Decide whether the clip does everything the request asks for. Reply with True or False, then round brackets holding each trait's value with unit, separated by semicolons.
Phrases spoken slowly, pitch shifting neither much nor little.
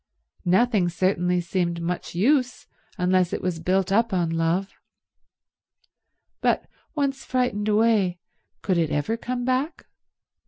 True (120 wpm; 4.9 semitones)